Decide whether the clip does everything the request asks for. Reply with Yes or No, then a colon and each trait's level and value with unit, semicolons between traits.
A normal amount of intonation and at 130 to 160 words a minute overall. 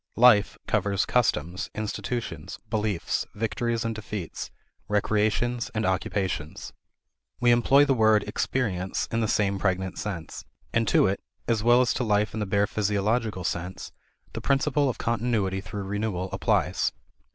Yes: average, 3.2 semitones; average, 140 wpm